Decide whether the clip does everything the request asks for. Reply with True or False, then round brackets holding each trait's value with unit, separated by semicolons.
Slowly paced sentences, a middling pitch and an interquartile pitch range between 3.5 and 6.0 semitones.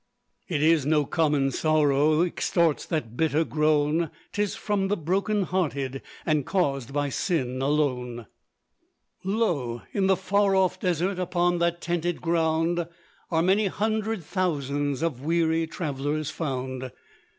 True (130 wpm; 160 Hz; 4.0 semitones)